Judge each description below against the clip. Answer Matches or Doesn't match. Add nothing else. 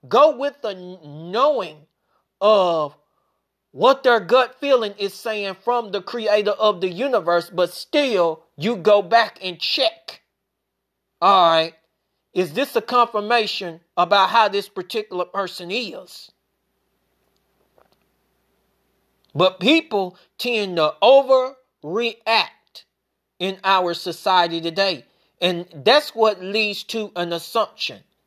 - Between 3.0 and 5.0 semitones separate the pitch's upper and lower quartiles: Matches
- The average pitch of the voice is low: Doesn't match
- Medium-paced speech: Doesn't match